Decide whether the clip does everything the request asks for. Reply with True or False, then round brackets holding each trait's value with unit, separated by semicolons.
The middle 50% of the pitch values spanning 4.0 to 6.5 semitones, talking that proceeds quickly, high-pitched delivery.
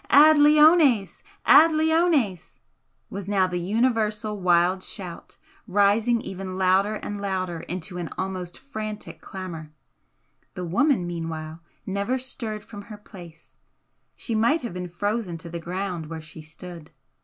False (4.4 semitones; 135 wpm; 195 Hz)